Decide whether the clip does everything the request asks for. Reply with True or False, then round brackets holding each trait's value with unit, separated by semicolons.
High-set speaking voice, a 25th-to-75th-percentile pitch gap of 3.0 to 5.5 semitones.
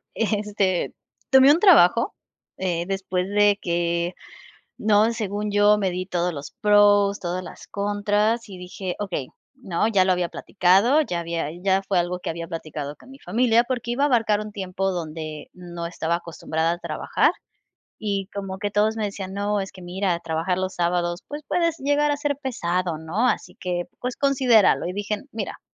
True (195 Hz; 3.5 semitones)